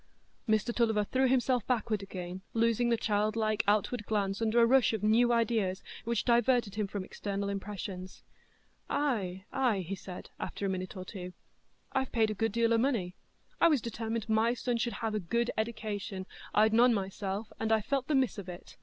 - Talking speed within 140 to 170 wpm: No, average, 180 wpm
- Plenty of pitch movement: No, average, 3.0 semitones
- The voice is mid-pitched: No, high, 220 Hz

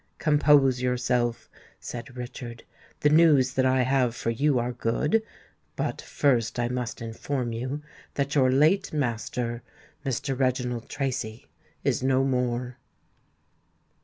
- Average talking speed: No, slow, 125 wpm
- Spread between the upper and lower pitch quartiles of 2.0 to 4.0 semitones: Yes, narrow, 2.4 semitones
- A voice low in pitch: Yes, low, 125 Hz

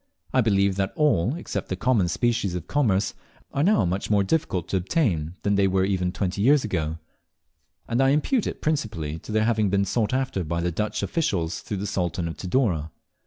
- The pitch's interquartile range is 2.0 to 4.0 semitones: No, average, 5.1 semitones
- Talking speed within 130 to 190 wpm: No, average, 200 wpm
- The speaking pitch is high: No, low, 100 Hz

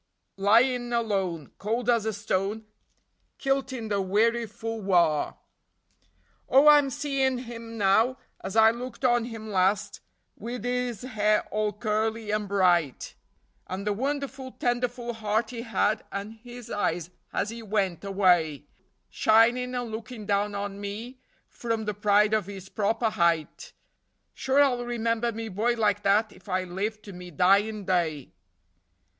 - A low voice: No, high, 220 Hz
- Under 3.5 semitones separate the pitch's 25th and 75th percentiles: Yes, average, 3.1 semitones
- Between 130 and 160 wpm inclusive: Yes, average, 145 wpm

